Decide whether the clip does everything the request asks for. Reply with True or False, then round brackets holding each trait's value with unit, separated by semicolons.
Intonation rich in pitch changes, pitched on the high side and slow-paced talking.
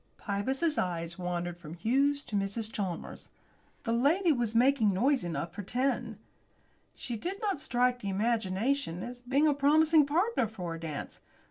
False (6.9 semitones; 235 Hz; 155 wpm)